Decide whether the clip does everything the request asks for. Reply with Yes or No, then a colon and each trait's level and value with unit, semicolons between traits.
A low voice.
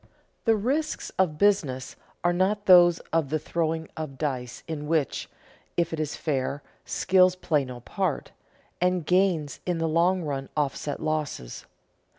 No: medium, 160 Hz